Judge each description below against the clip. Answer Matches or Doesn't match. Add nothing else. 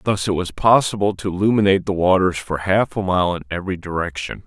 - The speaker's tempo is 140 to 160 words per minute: Doesn't match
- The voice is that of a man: Matches